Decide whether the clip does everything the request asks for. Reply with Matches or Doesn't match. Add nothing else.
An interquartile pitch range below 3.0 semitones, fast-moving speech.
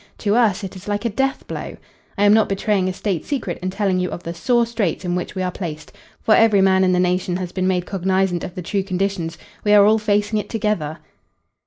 Matches